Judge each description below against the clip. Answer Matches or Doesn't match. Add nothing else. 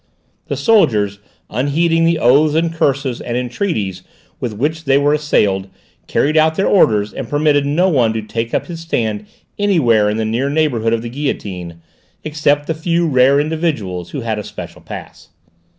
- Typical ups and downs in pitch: Doesn't match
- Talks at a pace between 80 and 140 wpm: Doesn't match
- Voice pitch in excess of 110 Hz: Matches